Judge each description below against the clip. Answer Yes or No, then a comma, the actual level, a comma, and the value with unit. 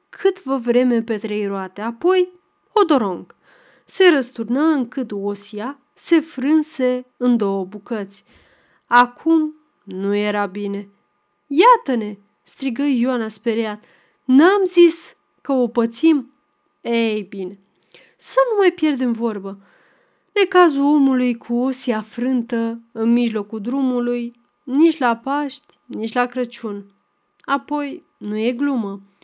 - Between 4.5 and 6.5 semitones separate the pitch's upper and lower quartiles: Yes, average, 5.3 semitones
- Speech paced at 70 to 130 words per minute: Yes, slow, 115 wpm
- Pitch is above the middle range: Yes, high, 245 Hz